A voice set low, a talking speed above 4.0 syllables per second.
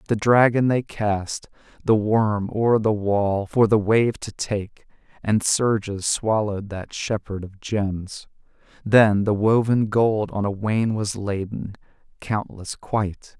No: low, 105 Hz; 3.7 syllables/s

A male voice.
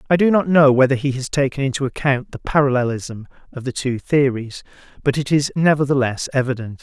Yes: male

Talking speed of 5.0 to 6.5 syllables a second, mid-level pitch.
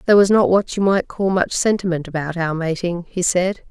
Yes: 5.4 syllables/s; medium, 180 Hz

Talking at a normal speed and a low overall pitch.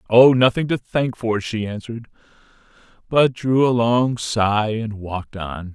Yes: average, 155 wpm; low, 115 Hz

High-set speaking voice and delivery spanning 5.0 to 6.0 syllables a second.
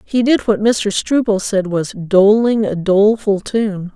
No: high, 210 Hz; 3.9 syllables/s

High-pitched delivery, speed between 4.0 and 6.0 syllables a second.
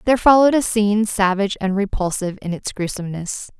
No: high, 205 Hz; 6.5 syllables/s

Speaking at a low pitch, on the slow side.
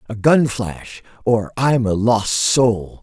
Yes: low, 115 Hz; slow, 120 wpm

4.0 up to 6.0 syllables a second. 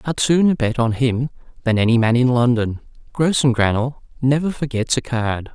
Yes: 5.1 syllables/s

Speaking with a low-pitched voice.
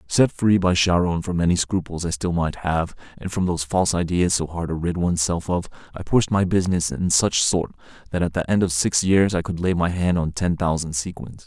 Yes: very low, 85 Hz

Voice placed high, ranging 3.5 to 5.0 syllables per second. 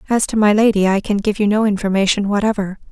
No: high, 205 Hz; 6.5 syllables/s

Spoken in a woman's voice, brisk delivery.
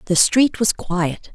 No: female; average, 180 wpm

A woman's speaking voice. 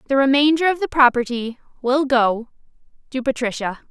Yes: female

